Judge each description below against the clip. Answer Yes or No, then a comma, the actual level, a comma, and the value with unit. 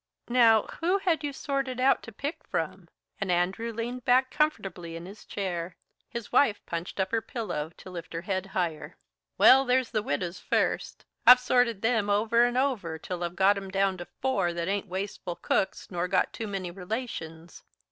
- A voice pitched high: Yes, high, 200 Hz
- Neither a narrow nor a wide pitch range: No, wide, 5.7 semitones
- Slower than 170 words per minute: No, average, 185 wpm